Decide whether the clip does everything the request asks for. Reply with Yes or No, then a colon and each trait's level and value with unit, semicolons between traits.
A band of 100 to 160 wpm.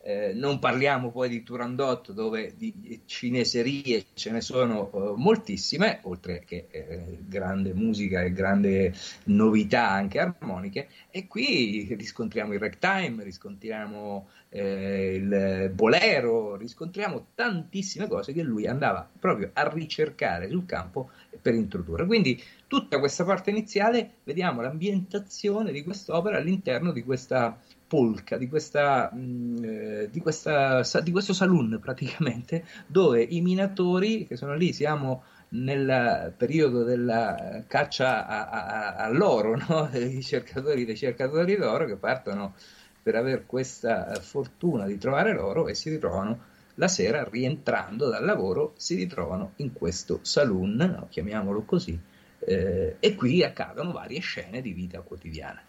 Yes: average, 130 wpm